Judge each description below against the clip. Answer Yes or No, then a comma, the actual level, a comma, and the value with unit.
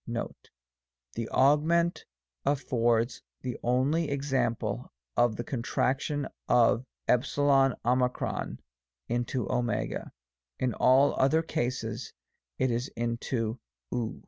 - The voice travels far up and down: No, narrow, 2.6 semitones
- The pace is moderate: No, slow, 90 wpm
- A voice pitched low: Yes, low, 125 Hz